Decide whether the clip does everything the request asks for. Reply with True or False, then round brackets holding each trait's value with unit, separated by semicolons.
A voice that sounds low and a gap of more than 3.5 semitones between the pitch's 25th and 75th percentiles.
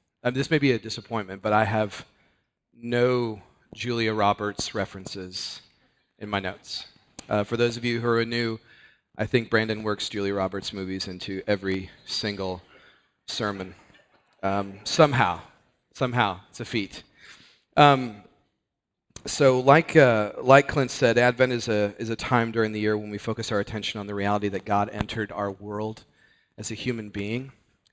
False (110 Hz; 2.7 semitones)